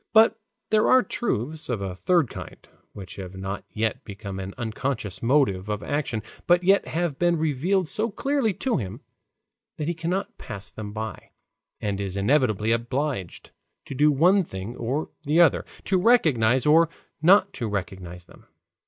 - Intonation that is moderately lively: No, wide, 9.0 semitones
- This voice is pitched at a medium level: No, low, 130 Hz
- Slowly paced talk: No, average, 160 wpm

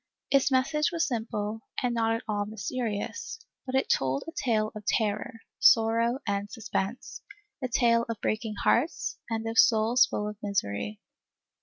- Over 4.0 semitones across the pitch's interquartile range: No, average, 2.9 semitones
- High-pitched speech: Yes, high, 225 Hz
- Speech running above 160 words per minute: No, average, 155 wpm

